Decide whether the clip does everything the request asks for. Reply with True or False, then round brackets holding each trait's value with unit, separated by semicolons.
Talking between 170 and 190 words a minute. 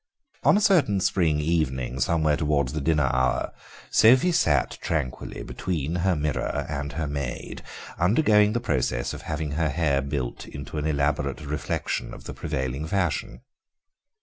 False (150 wpm)